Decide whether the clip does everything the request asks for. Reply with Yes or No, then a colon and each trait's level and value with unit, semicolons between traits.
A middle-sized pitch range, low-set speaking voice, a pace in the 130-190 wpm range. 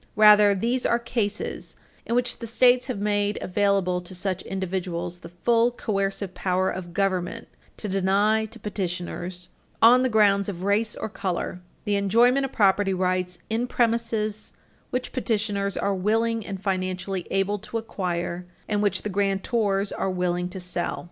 No: average, 3.0 semitones; high, 200 Hz; average, 155 wpm